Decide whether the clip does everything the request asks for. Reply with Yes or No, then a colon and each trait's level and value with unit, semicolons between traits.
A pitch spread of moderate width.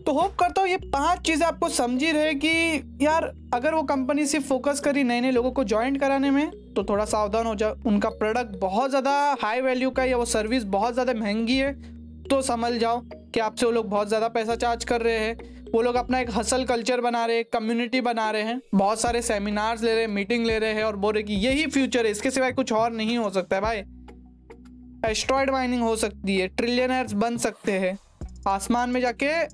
Yes: average, 3.4 semitones